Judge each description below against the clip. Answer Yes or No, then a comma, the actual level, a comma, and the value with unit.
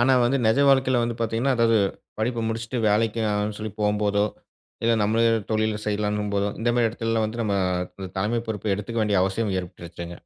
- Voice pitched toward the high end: No, low, 110 Hz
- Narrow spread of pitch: Yes, narrow, 1.9 semitones